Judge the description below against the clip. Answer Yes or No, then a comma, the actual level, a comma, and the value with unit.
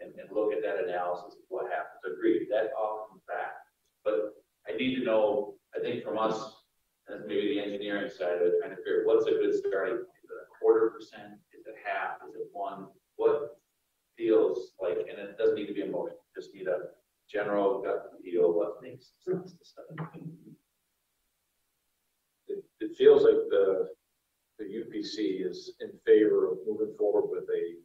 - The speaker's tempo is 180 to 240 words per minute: Yes, average, 185 wpm